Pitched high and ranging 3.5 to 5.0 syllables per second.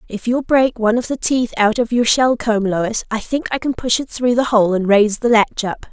No: high, 230 Hz; 5.2 syllables/s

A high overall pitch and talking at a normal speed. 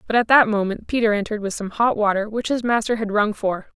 No: high, 215 Hz; fast, 255 wpm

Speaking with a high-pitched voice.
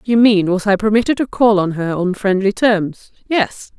Yes: high, 205 Hz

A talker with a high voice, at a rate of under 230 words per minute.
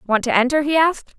No: very high, 275 Hz; fast, 255 wpm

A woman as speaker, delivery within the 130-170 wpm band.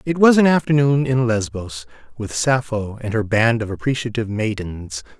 No: male; average, 150 wpm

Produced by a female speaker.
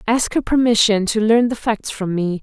Yes: female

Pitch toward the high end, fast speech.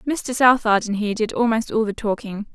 Yes: high, 220 Hz; fast, 215 wpm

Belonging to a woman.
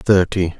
No: male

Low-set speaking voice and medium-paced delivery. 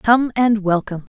No: high, 210 Hz; average, 160 wpm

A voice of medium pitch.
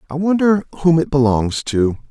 Yes: medium, 145 Hz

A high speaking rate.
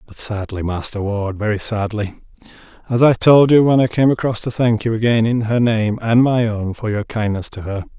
Yes: fast, 220 wpm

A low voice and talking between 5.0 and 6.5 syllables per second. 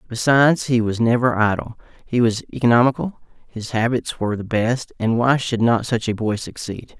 Yes: low, 115 Hz; 5.2 syllables/s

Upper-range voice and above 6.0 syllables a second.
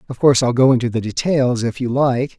No: low, 125 Hz; 6.3 syllables/s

